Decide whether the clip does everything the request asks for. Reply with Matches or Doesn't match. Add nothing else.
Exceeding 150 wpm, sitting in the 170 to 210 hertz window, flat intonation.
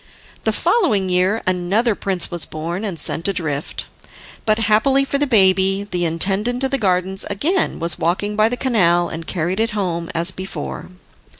Doesn't match